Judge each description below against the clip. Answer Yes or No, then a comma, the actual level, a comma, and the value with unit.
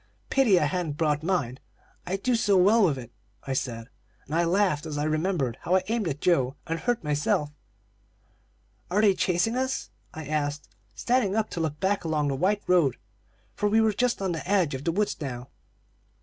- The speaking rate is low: No, average, 195 wpm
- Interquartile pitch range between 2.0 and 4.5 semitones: No, wide, 5.5 semitones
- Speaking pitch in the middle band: Yes, medium, 170 Hz